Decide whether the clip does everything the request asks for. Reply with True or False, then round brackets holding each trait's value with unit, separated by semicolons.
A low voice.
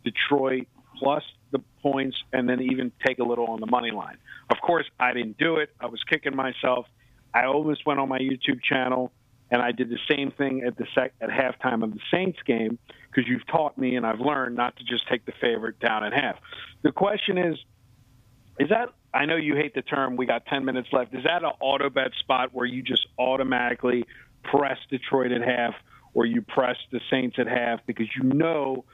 True (130 Hz)